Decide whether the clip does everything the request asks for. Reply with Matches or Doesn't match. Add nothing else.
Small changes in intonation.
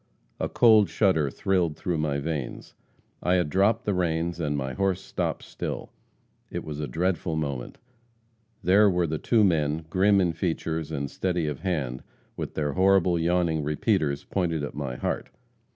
Doesn't match